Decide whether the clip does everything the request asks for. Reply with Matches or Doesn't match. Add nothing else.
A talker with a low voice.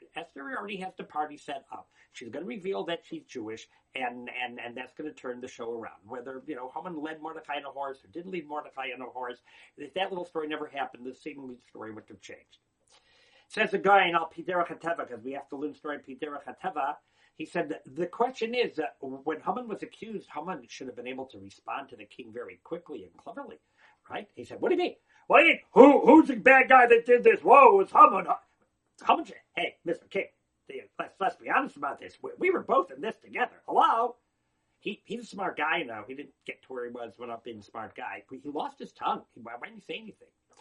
Doesn't match